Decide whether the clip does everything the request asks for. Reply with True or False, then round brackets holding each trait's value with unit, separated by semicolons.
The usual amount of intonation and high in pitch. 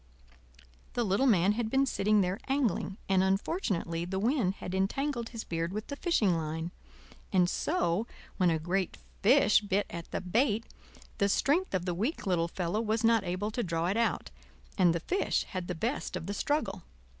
True (4.6 semitones; 195 Hz)